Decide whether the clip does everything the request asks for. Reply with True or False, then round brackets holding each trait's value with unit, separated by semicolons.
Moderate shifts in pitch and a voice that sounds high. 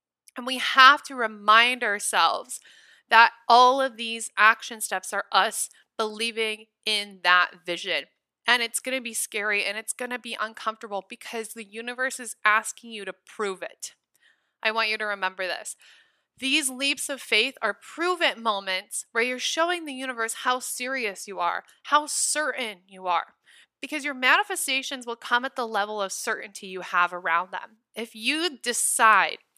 True (3.9 semitones; 230 Hz)